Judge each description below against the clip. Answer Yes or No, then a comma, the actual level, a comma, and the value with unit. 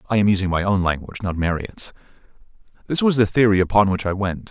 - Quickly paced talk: Yes, fast, 215 wpm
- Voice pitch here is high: No, low, 100 Hz